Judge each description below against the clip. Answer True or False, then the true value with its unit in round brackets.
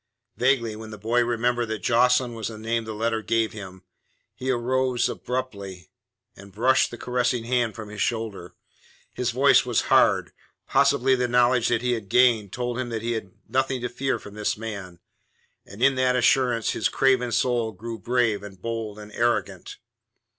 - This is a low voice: True (120 Hz)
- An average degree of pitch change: False (2.3 semitones)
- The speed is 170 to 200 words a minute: True (175 wpm)